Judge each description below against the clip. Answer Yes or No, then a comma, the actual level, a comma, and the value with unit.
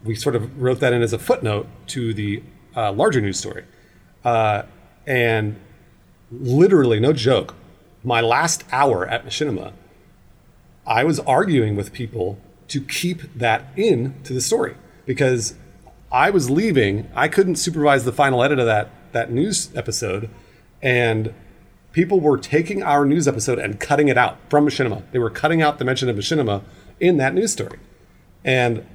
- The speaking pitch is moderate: No, low, 120 Hz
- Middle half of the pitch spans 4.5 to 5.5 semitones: Yes, average, 5.2 semitones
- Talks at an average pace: Yes, average, 160 wpm